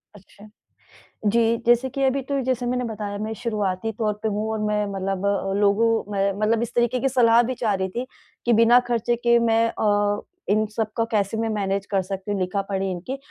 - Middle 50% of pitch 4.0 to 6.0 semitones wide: No, average, 2.9 semitones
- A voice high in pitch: Yes, high, 220 Hz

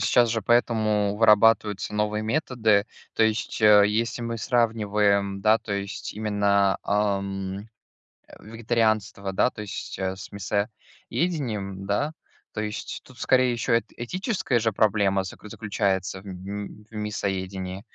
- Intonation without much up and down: Yes, narrow, 2.3 semitones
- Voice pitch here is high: No, low, 105 Hz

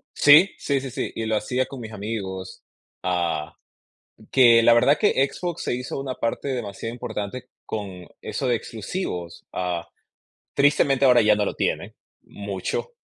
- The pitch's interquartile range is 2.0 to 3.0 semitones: No, average, 4.8 semitones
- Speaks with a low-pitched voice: Yes, low, 115 Hz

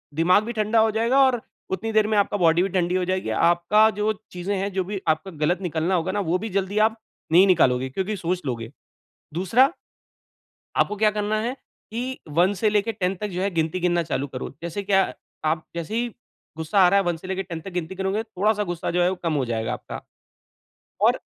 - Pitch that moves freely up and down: No, average, 3.6 semitones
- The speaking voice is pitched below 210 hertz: Yes, high, 190 Hz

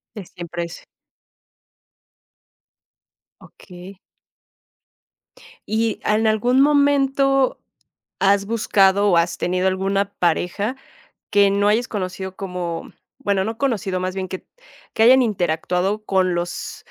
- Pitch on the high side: Yes, high, 200 Hz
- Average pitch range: Yes, average, 3.3 semitones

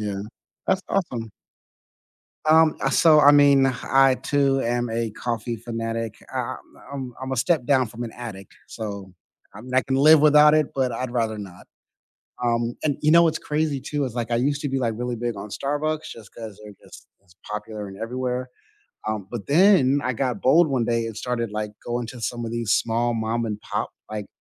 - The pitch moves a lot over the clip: No, average, 3.5 semitones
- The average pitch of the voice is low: Yes, low, 120 Hz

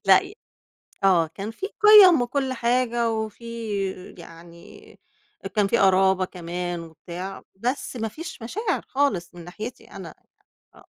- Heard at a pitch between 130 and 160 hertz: No, high, 215 Hz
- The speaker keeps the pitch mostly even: No, wide, 5.6 semitones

